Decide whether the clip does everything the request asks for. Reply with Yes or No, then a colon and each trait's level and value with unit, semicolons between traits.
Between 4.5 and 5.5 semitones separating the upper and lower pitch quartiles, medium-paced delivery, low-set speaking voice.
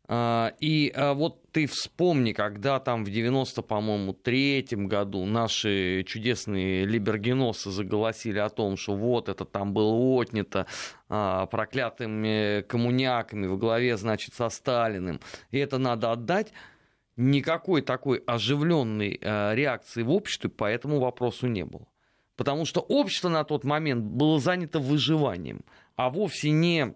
Yes: average, 4.9 semitones; average, 125 wpm; low, 120 Hz